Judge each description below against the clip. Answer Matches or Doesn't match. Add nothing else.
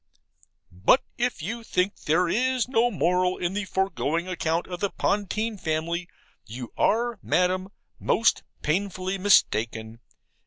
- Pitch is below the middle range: Doesn't match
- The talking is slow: Matches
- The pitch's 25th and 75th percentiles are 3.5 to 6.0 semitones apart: Matches